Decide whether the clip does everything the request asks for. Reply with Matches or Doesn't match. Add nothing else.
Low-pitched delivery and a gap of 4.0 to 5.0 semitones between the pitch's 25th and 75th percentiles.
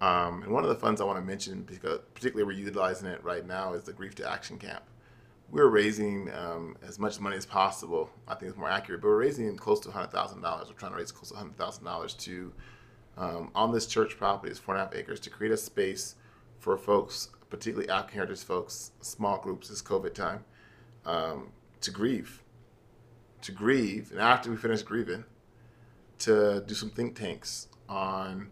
Doesn't match